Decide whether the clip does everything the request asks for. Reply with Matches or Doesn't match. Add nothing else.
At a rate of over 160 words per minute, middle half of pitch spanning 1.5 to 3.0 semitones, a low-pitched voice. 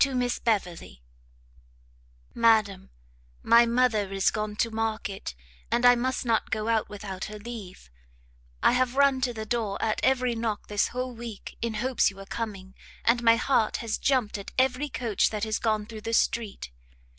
Doesn't match